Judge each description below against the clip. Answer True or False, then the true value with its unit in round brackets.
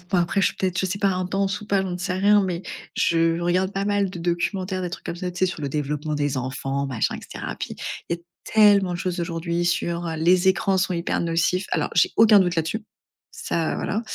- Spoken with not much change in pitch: True (2.3 semitones)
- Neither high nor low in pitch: True (180 Hz)